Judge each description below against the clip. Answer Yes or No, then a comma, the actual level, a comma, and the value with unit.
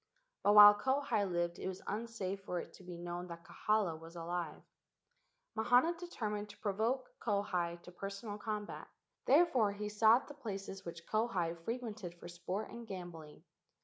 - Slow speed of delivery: No, average, 165 wpm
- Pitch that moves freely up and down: No, average, 4.1 semitones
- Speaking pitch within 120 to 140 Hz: No, high, 200 Hz